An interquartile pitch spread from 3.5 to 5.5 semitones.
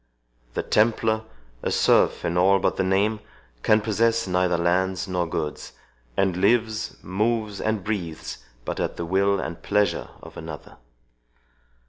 No: average, 3.1 semitones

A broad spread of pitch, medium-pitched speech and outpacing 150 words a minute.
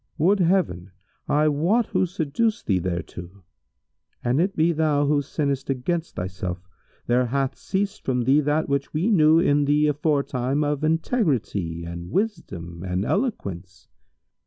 No: wide, 8.6 semitones; medium, 145 Hz; average, 140 wpm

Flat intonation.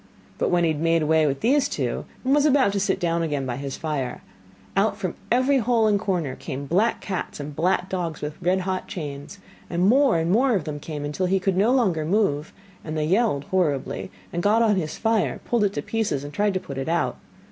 No: wide, 5.5 semitones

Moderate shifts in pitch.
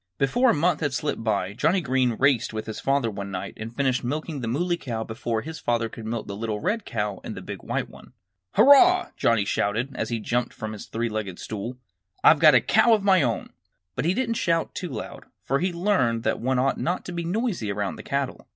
No: wide, 7.4 semitones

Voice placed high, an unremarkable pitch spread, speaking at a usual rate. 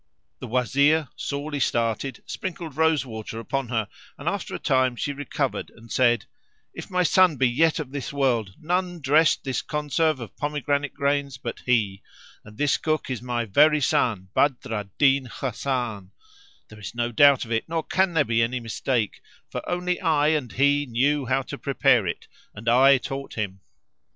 No: low, 135 Hz; average, 4.1 semitones; average, 175 wpm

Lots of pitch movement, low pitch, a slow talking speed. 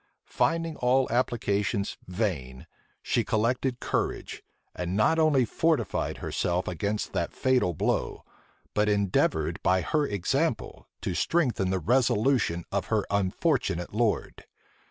Yes: wide, 5.7 semitones; low, 110 Hz; slow, 115 wpm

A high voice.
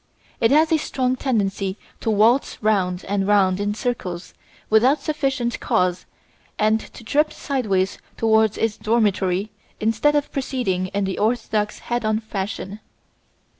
Yes: high, 215 Hz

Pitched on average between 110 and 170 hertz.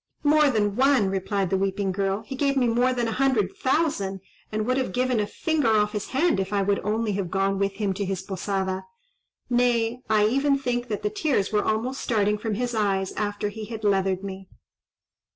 No: high, 210 Hz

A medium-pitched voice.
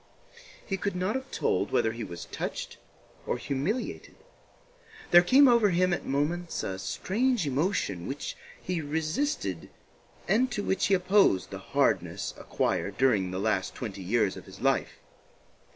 Yes: medium, 160 Hz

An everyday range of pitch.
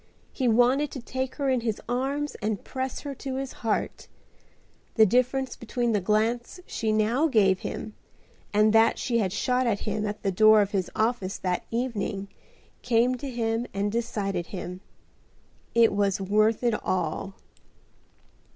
Yes: average, 3.4 semitones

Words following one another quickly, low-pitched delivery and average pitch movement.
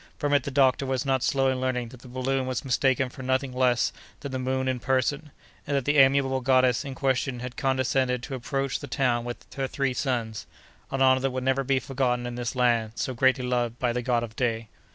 No: fast, 225 wpm; low, 130 Hz; narrow, 1.5 semitones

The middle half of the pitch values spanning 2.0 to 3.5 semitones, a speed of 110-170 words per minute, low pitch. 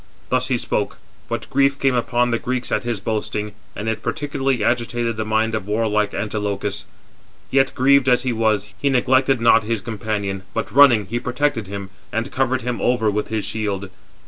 No: average, 3.2 semitones; average, 180 wpm; low, 115 Hz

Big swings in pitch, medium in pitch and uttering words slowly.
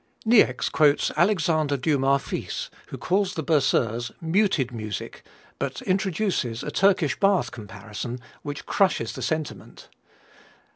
Yes: wide, 7.0 semitones; medium, 150 Hz; slow, 115 wpm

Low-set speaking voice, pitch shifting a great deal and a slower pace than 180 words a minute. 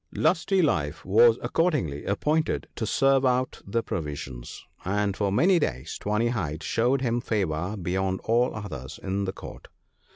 Yes: low, 105 Hz; wide, 5.7 semitones; average, 155 wpm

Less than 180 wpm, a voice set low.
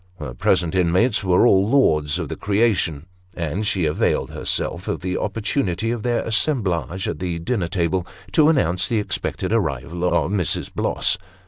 Yes: average, 160 wpm; very low, 95 Hz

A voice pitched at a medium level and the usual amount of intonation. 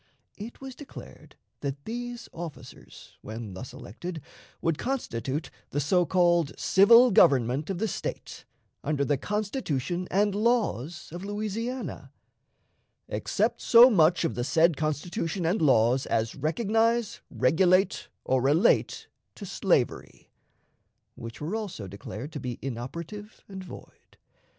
No: medium, 170 Hz; wide, 7.2 semitones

